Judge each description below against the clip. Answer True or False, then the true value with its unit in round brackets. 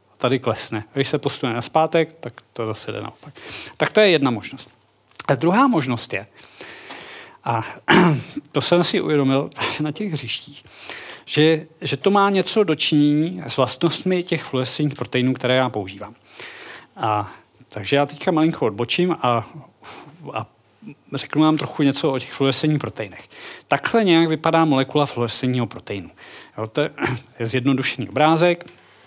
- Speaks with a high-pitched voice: False (140 Hz)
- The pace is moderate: True (145 wpm)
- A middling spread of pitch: True (4.5 semitones)